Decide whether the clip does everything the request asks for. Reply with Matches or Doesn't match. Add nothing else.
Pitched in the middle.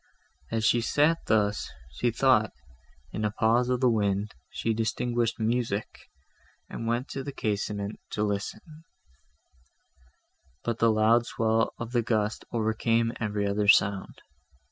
Doesn't match